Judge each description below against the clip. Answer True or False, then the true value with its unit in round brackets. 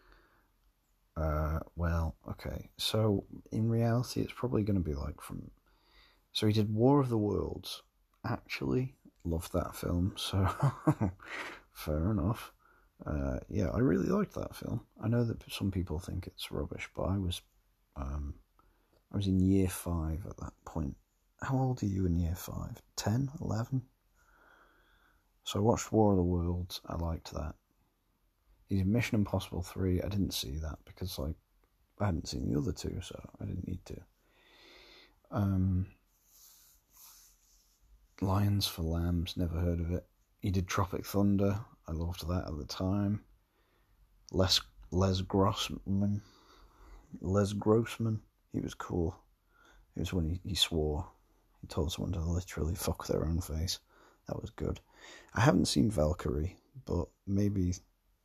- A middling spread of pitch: True (3.1 semitones)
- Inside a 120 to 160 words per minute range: True (150 wpm)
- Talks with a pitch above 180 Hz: False (95 Hz)